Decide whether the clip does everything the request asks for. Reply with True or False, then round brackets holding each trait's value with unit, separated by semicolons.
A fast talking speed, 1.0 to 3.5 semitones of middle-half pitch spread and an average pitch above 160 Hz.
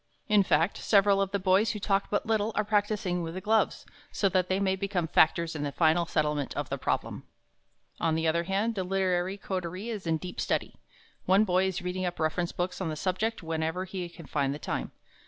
True (215 wpm; 3.0 semitones; 185 Hz)